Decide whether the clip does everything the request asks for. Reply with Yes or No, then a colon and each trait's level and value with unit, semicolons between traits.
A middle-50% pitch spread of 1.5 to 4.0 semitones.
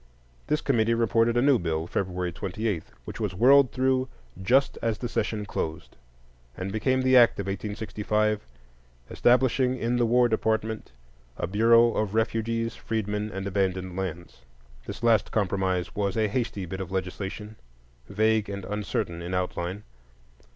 Yes: average, 3.4 semitones